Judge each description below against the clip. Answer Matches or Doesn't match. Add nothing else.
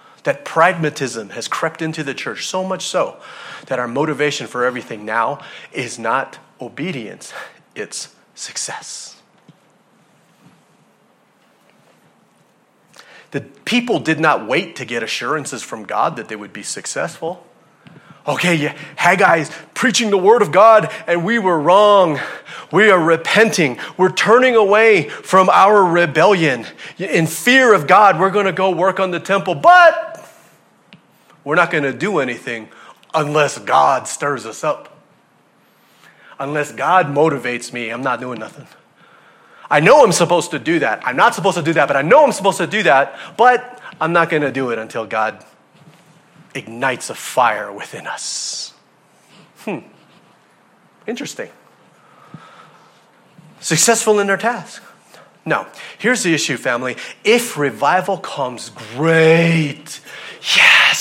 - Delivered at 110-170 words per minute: Matches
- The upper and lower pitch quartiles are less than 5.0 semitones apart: Doesn't match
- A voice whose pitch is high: Doesn't match